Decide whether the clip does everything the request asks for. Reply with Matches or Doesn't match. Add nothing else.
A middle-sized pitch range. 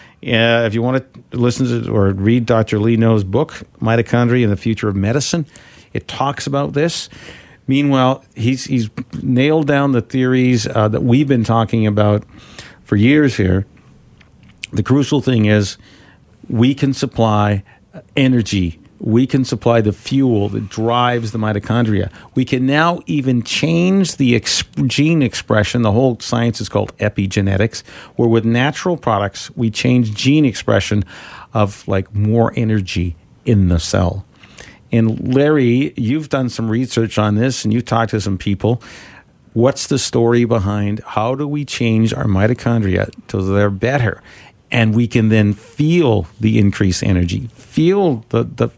Matches